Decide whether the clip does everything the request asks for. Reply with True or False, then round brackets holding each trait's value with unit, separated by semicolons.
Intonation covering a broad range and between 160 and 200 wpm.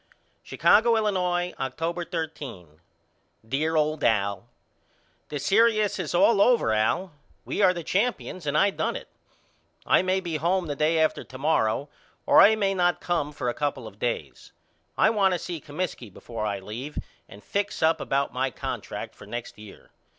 True (6.7 semitones; 170 wpm)